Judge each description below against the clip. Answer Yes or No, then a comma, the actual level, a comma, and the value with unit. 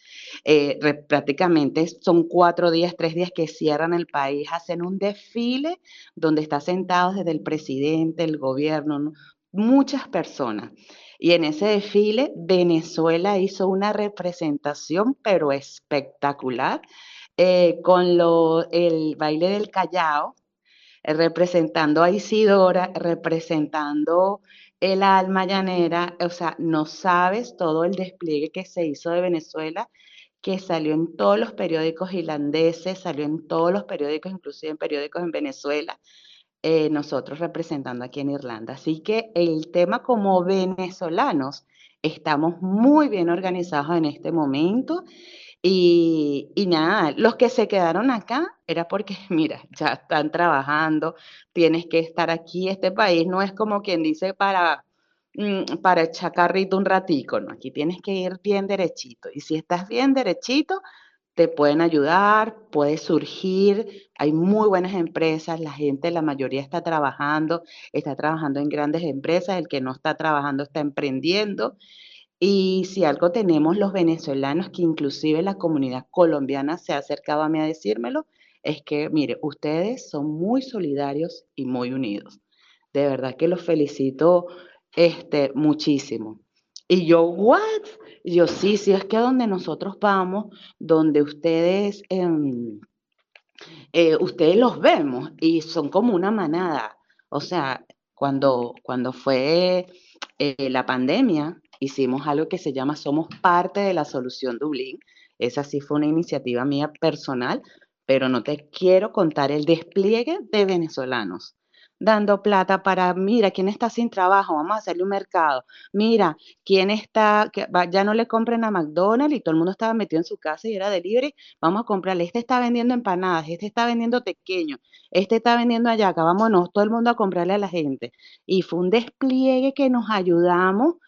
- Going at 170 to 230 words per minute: No, average, 150 wpm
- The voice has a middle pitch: Yes, medium, 170 Hz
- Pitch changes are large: No, average, 4.3 semitones